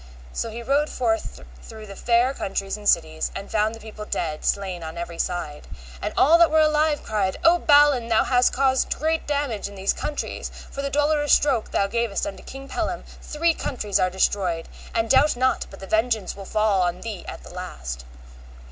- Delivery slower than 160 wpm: No, average, 195 wpm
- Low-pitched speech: No, high, 225 Hz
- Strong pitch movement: Yes, wide, 6.5 semitones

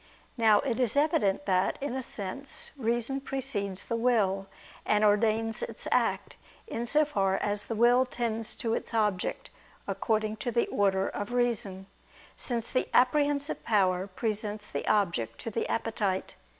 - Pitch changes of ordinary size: Yes, average, 3.3 semitones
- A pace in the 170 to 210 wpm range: No, average, 150 wpm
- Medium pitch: No, high, 225 Hz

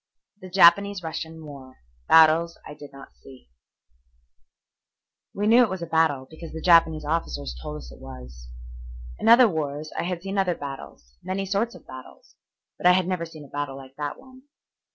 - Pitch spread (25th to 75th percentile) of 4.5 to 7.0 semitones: Yes, average, 5.0 semitones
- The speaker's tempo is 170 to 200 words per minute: Yes, average, 180 wpm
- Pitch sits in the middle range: Yes, medium, 160 Hz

